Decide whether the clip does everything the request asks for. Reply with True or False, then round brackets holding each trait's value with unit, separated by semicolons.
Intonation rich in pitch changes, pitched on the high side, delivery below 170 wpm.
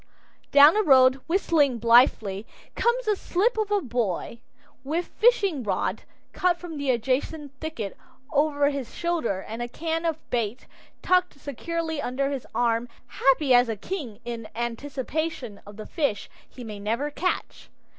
True (5.7 semitones; 275 Hz; 150 wpm)